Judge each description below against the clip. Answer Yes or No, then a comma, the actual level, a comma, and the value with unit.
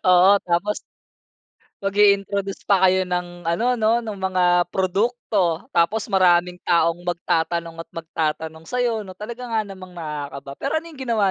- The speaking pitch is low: No, medium, 185 Hz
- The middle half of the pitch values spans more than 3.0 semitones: Yes, average, 3.4 semitones